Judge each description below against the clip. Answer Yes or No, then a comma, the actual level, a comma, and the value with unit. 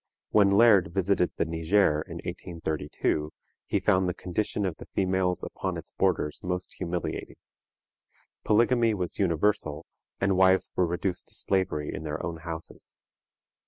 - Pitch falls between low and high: No, very low, 90 Hz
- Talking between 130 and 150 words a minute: Yes, average, 140 wpm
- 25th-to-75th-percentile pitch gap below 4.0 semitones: Yes, average, 3.1 semitones